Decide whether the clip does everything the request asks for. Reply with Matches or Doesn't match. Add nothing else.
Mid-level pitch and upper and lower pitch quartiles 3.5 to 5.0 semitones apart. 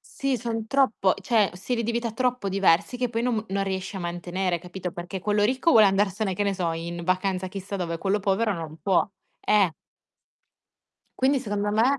Doesn't match